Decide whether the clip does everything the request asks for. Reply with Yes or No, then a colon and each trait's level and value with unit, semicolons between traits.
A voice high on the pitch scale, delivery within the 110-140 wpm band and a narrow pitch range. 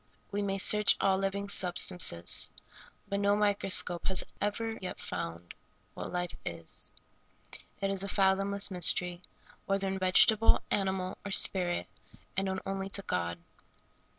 Yes: high, 195 Hz; slow, 135 wpm; narrow, 1.8 semitones